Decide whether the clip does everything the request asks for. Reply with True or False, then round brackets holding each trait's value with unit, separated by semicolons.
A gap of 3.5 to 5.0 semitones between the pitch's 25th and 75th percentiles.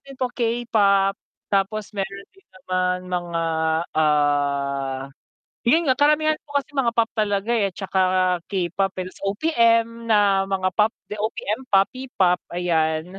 True (4.2 semitones)